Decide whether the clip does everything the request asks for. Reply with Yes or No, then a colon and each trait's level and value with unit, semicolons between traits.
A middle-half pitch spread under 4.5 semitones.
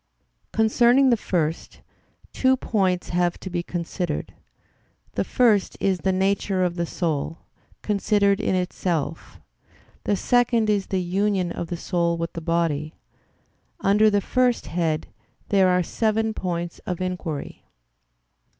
Yes: average, 3.4 semitones